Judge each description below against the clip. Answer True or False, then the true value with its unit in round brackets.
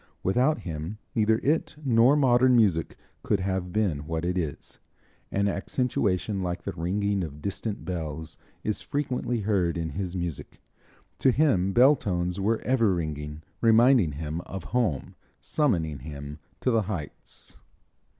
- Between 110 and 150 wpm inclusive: True (140 wpm)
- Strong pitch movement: True (5.8 semitones)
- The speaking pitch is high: False (95 Hz)